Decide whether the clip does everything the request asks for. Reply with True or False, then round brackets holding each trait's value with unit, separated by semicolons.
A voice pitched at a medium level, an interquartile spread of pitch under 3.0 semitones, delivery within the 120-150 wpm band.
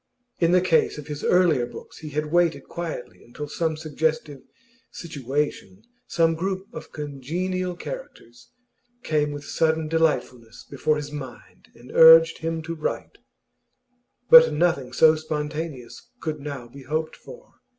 True (155 Hz; 2.4 semitones; 140 wpm)